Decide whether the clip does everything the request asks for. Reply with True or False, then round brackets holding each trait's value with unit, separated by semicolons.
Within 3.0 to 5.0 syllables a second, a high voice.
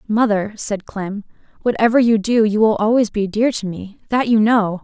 True (4.8 syllables/s; 215 Hz)